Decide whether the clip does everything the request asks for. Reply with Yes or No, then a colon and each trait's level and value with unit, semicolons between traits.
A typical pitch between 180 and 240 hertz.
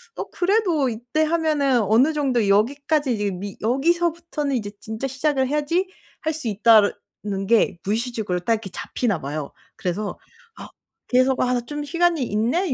No: very high, 250 Hz